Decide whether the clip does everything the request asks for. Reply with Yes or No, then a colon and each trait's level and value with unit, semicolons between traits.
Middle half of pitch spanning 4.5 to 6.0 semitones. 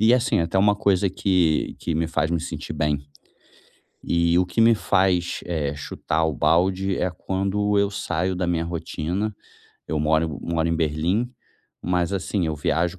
No: average, 3.1 semitones